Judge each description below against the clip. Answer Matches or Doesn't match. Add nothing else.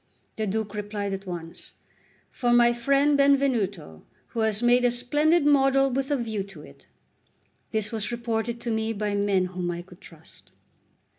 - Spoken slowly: Doesn't match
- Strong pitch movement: Doesn't match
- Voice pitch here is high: Matches